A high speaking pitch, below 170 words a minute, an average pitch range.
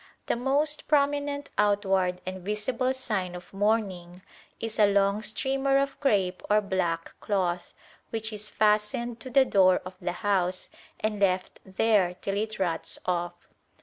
Yes: high, 205 Hz; average, 150 wpm; average, 4.3 semitones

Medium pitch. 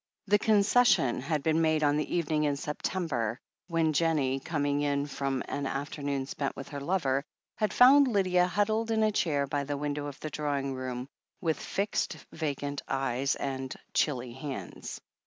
Yes: medium, 145 Hz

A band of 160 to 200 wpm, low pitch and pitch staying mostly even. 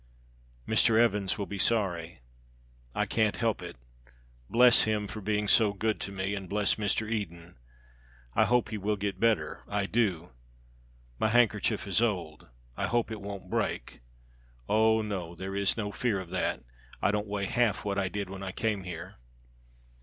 Yes: average, 170 wpm; low, 105 Hz; narrow, 2.3 semitones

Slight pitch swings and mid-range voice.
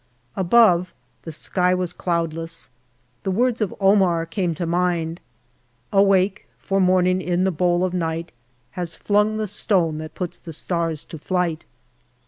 Yes: narrow, 2.3 semitones; medium, 180 Hz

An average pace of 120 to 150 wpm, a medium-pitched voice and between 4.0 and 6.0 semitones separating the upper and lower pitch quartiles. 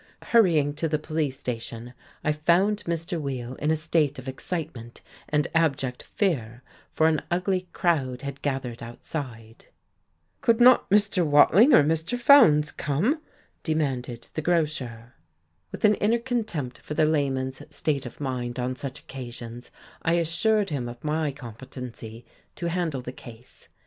Yes: average, 145 wpm; medium, 150 Hz; average, 5.0 semitones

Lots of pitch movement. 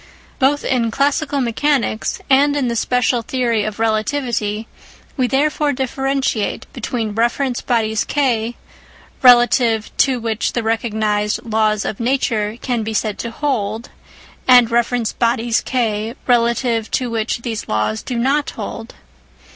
No: average, 2.9 semitones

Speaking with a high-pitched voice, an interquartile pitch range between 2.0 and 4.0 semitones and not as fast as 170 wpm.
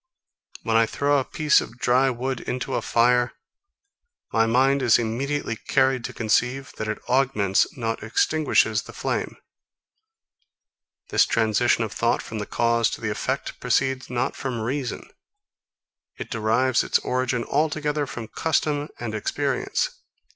No: low, 125 Hz; average, 3.1 semitones; average, 140 wpm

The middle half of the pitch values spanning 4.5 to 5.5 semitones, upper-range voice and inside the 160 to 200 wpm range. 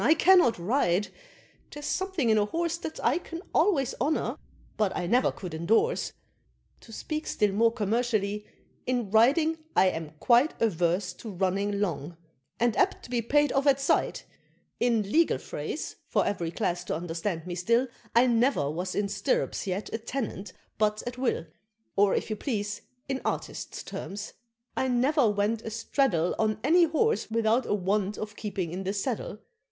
Yes: average, 5.2 semitones; high, 220 Hz; average, 170 wpm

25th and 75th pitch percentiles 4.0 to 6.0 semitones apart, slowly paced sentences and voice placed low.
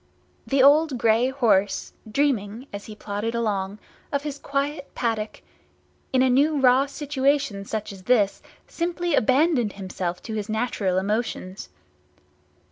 No: average, 5.3 semitones; slow, 130 wpm; high, 240 Hz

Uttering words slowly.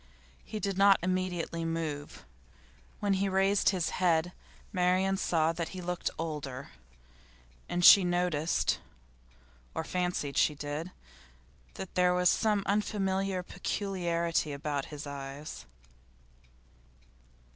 Yes: slow, 110 wpm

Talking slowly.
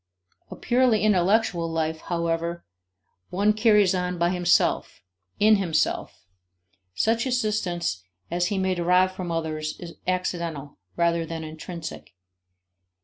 Yes: slow, 115 wpm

